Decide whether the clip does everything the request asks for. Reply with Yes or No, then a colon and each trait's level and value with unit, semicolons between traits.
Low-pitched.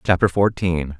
Yes: very low, 90 Hz